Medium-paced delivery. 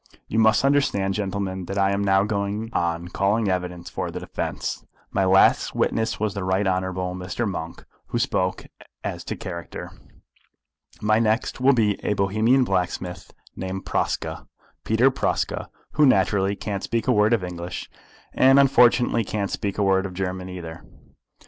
Yes: average, 160 wpm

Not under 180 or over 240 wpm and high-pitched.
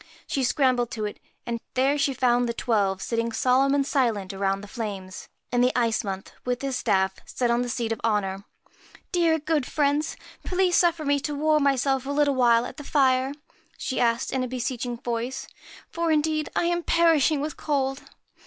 Yes: average, 195 wpm; very high, 255 Hz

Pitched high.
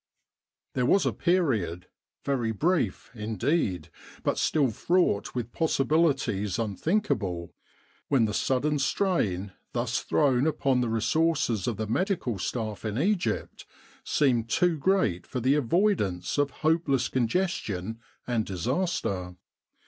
No: low, 125 Hz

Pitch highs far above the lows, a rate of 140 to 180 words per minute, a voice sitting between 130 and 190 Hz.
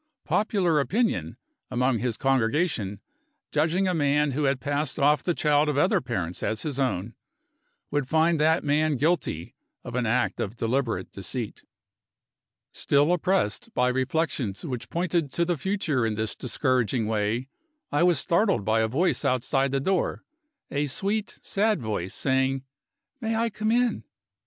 Yes: wide, 5.7 semitones; average, 150 wpm; medium, 140 Hz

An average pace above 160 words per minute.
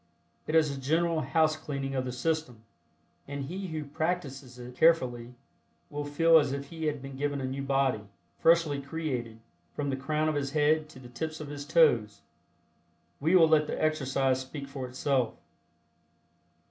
Yes: average, 170 wpm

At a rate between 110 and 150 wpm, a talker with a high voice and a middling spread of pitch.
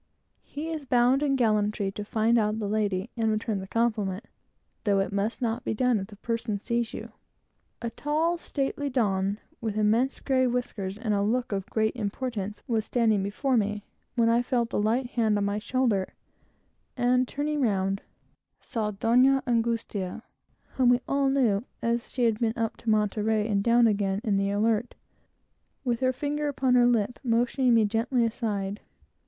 No: average, 175 wpm; high, 230 Hz; average, 3.1 semitones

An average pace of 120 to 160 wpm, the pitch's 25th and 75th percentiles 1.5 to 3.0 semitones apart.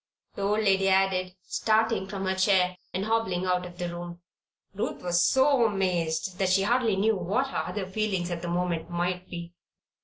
No: average, 185 wpm; average, 2.7 semitones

